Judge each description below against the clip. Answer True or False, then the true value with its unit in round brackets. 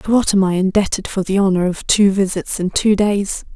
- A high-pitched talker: True (195 Hz)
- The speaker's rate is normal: False (235 wpm)